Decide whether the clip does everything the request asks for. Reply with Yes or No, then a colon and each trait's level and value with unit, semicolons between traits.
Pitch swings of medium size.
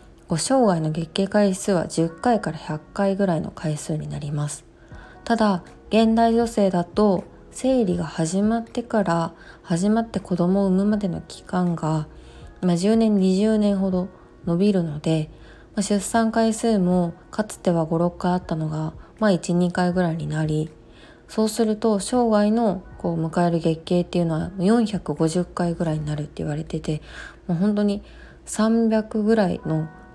Yes: average, 4.4 semitones